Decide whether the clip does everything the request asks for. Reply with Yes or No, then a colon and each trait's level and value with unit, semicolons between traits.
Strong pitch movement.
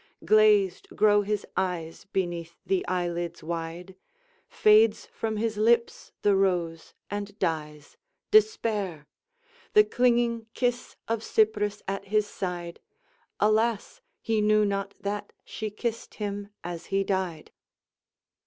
No: average, 3.4 semitones